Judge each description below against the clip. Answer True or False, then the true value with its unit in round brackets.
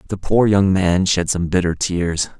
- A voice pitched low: True (90 Hz)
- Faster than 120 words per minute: True (200 wpm)